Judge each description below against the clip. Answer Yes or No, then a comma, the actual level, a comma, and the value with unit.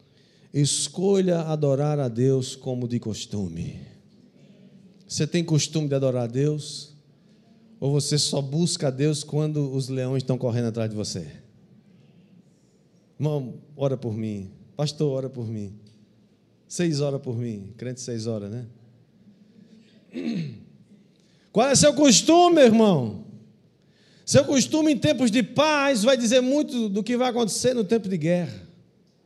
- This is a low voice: No, medium, 150 Hz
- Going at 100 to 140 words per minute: Yes, average, 135 wpm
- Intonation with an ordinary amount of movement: No, wide, 8.0 semitones